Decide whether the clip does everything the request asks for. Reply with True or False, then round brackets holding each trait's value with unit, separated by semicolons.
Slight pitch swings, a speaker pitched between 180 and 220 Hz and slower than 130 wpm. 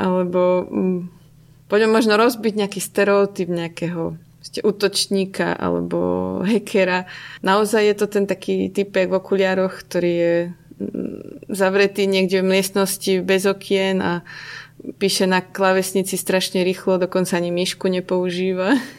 True (1.9 semitones; 190 Hz; 115 wpm)